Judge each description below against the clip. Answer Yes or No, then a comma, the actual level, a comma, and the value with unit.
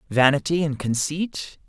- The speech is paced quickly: No, slow, 105 wpm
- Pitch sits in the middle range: Yes, medium, 150 Hz